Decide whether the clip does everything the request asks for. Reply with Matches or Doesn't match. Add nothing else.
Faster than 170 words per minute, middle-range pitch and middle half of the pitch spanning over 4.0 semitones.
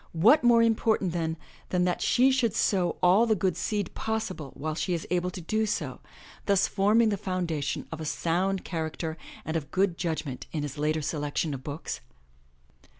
Matches